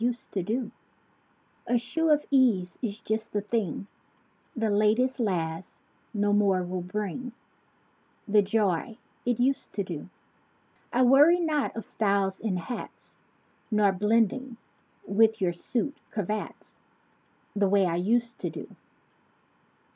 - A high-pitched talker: Yes, high, 215 Hz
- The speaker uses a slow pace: Yes, slow, 130 wpm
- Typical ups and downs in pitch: Yes, average, 3.9 semitones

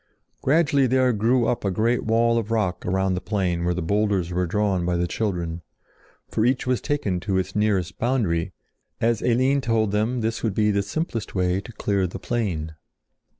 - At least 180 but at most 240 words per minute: Yes, average, 190 wpm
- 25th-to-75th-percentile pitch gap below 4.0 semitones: No, average, 4.3 semitones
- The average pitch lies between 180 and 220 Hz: No, low, 105 Hz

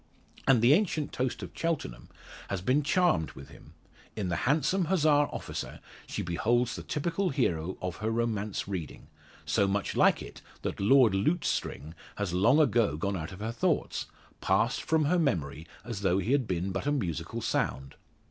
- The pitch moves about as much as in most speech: No, wide, 7.9 semitones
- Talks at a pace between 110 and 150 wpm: No, average, 175 wpm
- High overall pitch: No, low, 115 Hz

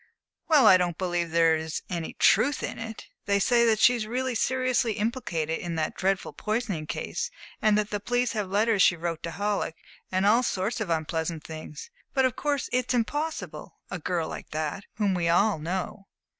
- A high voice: Yes, high, 200 Hz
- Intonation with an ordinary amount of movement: No, wide, 5.8 semitones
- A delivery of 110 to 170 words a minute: No, average, 185 wpm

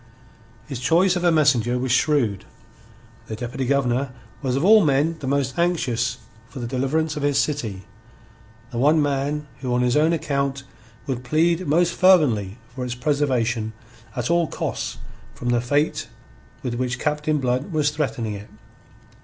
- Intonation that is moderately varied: Yes, average, 3.8 semitones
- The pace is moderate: Yes, average, 160 wpm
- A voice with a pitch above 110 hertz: Yes, medium, 140 Hz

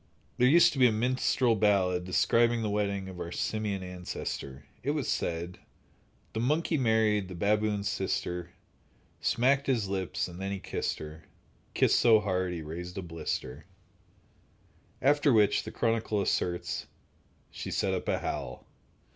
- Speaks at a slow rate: No, average, 150 wpm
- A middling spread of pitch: Yes, average, 4.4 semitones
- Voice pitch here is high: No, low, 100 Hz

